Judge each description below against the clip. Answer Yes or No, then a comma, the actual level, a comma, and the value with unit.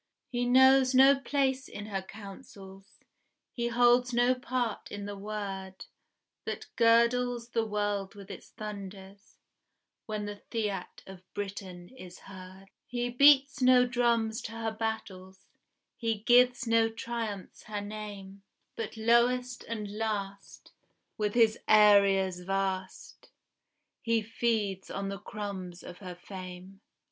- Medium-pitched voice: No, high, 215 Hz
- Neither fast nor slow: No, slow, 125 wpm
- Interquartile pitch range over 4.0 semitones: No, average, 3.5 semitones